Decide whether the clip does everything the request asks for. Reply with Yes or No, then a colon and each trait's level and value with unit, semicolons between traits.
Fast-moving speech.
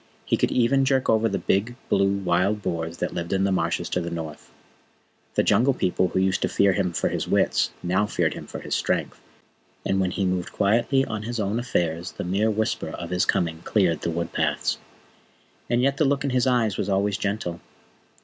Yes: fast, 210 wpm